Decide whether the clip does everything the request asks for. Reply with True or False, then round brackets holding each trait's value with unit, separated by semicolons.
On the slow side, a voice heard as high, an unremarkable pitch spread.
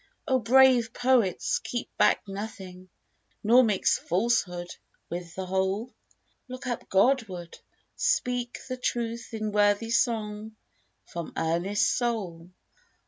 True (110 wpm; 215 Hz; 4.2 semitones)